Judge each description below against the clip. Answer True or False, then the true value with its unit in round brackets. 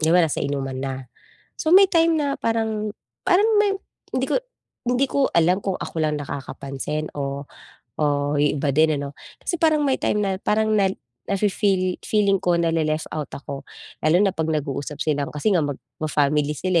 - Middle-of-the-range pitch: True (165 Hz)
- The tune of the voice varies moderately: False (6.6 semitones)